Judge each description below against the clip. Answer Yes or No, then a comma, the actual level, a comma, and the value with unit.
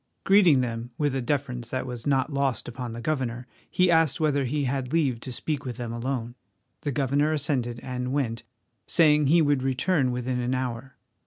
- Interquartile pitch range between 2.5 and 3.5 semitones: Yes, average, 2.9 semitones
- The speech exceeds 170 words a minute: Yes, average, 185 wpm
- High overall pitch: No, low, 130 Hz